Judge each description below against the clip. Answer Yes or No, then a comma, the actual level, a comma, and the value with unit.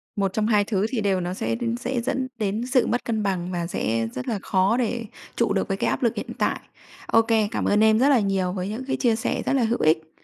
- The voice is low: No, high, 215 Hz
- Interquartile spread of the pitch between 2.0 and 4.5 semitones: Yes, average, 3.8 semitones